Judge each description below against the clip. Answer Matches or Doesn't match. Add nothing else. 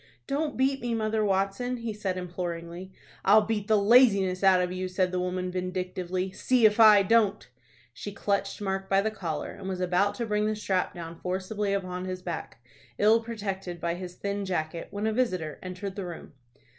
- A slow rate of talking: Doesn't match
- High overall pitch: Matches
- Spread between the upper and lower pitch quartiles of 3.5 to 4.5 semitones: Doesn't match